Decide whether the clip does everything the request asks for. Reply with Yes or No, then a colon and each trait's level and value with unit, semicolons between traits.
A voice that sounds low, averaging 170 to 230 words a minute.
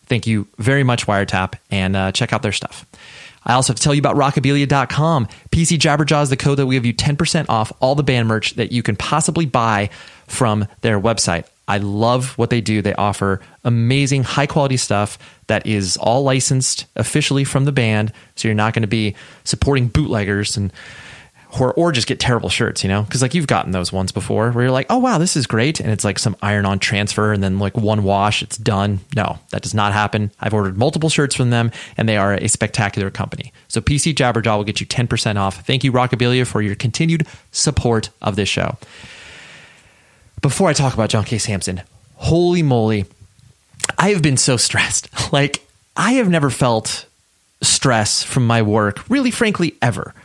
Yes: low, 115 Hz; average, 200 wpm